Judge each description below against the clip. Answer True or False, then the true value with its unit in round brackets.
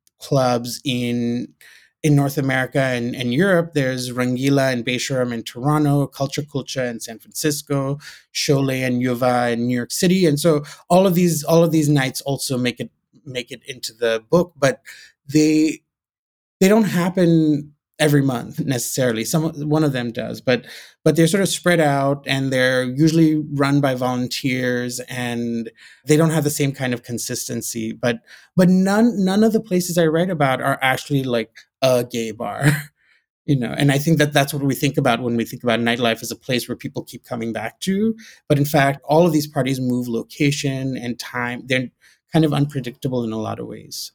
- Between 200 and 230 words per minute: False (190 wpm)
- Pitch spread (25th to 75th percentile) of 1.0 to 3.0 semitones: False (3.9 semitones)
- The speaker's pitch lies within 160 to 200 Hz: False (135 Hz)